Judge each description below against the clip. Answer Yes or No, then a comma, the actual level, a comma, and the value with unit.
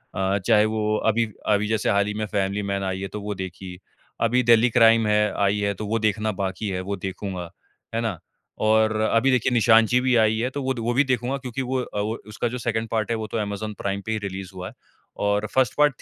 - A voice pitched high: No, low, 110 Hz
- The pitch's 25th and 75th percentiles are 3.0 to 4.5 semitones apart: No, narrow, 2.5 semitones